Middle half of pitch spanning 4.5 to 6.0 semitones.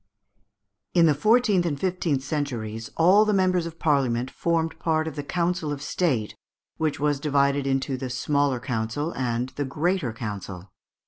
Yes: average, 4.9 semitones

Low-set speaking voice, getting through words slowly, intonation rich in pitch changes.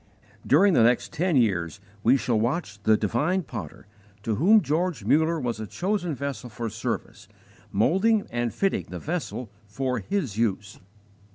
No: low, 125 Hz; average, 155 wpm; wide, 7.9 semitones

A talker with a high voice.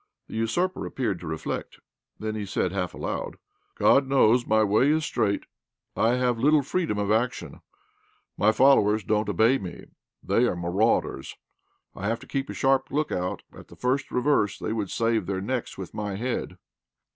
No: low, 110 Hz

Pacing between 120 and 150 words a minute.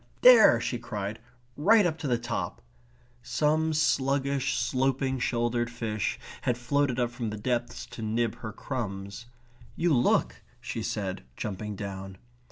Yes: average, 140 wpm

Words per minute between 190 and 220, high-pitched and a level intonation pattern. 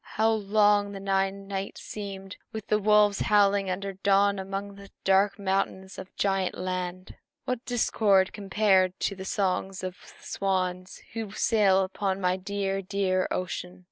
No: average, 155 wpm; high, 195 Hz; narrow, 1.2 semitones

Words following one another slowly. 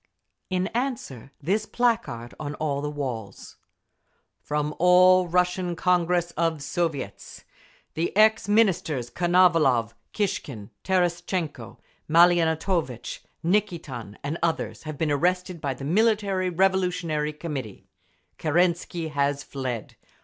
Yes: slow, 105 wpm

